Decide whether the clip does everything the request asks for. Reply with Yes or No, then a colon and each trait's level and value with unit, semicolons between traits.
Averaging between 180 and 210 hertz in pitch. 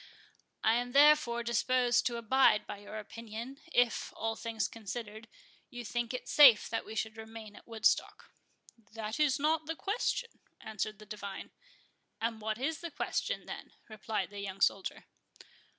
No: high, 225 Hz